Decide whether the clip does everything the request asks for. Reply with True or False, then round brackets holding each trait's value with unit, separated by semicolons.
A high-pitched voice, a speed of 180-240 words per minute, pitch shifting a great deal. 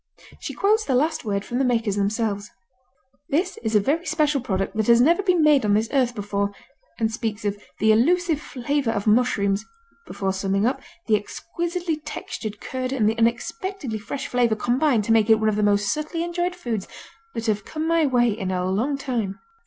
True (235 Hz; 195 wpm; 6.2 semitones)